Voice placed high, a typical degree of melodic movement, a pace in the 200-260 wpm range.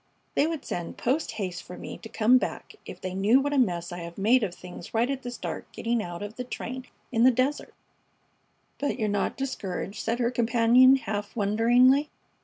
Yes: high, 230 Hz; average, 4.2 semitones; fast, 205 wpm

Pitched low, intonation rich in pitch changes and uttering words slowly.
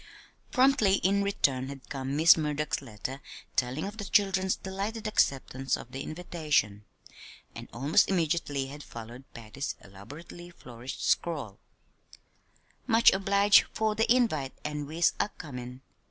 No: medium, 150 Hz; wide, 6.6 semitones; slow, 125 wpm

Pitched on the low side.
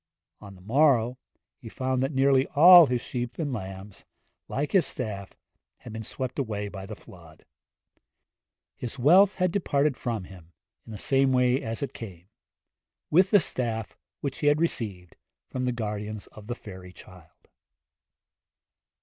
Yes: low, 120 Hz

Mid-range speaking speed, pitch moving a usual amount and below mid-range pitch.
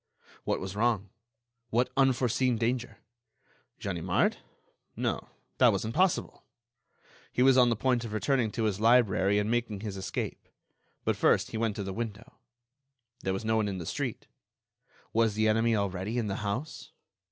Yes: average, 160 wpm; average, 3.1 semitones; low, 110 Hz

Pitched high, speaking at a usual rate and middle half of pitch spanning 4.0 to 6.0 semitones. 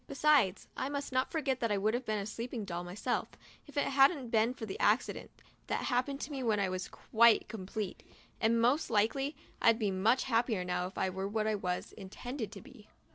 No: high, 225 Hz; fast, 220 wpm; average, 4.5 semitones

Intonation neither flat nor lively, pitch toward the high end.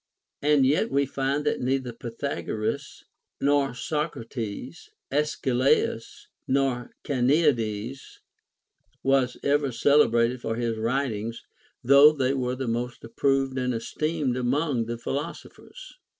No: average, 3.1 semitones; low, 130 Hz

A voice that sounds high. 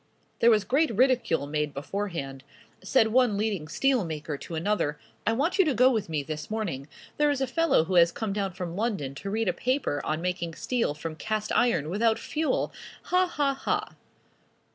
Yes: high, 205 Hz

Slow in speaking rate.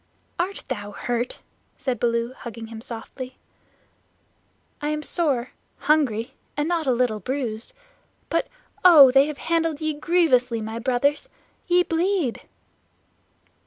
Yes: slow, 125 wpm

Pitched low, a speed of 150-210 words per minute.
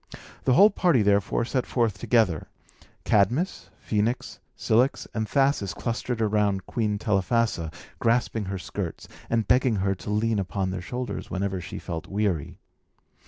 No: low, 105 Hz; average, 140 wpm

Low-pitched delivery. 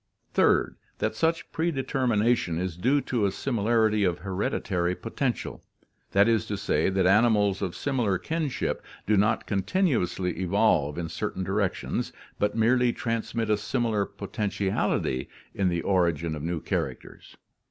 Yes: low, 105 Hz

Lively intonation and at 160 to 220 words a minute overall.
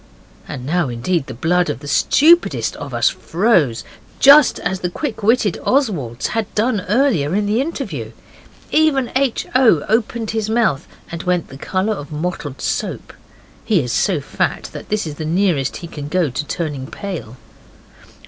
Yes: wide, 7.5 semitones; average, 165 wpm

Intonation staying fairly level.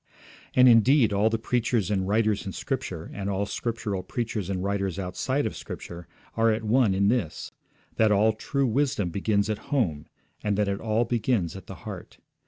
No: average, 3.0 semitones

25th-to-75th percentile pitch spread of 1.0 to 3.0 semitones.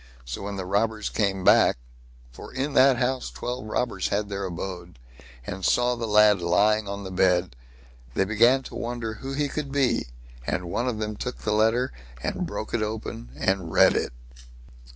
No: average, 4.9 semitones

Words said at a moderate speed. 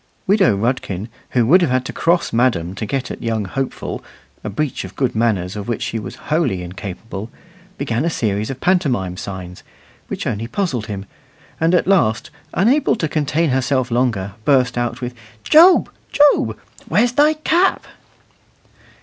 Yes: average, 160 wpm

